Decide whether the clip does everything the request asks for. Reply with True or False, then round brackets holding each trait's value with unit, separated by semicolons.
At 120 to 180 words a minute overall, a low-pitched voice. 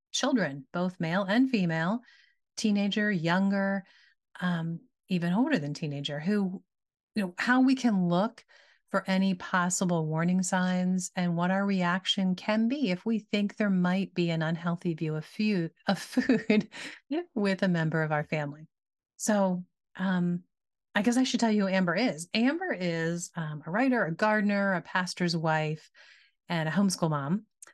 False (155 wpm; 185 Hz)